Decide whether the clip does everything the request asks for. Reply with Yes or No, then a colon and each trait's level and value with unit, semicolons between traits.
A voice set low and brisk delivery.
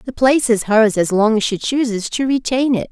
No: high, 235 Hz; fast, 245 wpm